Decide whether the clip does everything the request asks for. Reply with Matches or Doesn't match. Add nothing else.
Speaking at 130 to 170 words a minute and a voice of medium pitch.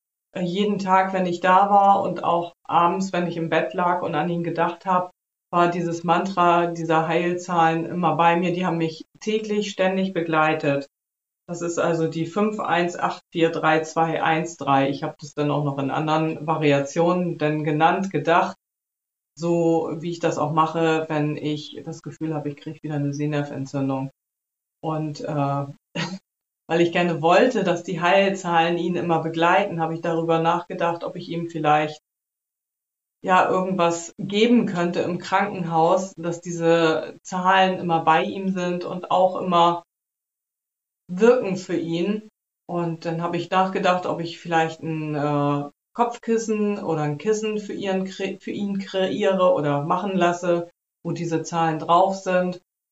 Matches